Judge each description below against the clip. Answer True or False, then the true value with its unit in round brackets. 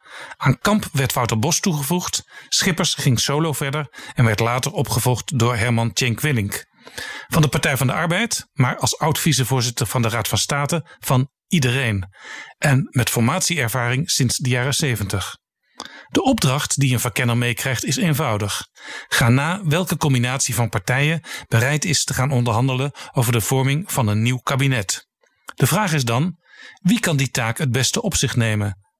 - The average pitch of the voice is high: False (130 Hz)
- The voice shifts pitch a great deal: False (4.2 semitones)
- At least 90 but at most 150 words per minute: False (165 wpm)